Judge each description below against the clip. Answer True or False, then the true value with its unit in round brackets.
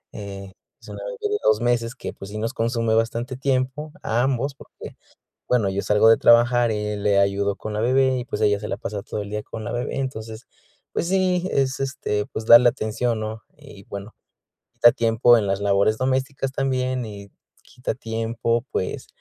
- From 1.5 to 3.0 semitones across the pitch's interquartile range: False (3.6 semitones)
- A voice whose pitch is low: True (115 Hz)